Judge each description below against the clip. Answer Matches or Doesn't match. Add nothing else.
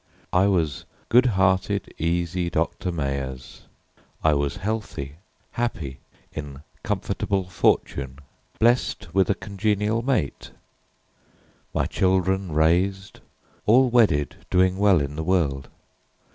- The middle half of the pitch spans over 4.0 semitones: Matches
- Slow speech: Matches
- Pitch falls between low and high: Doesn't match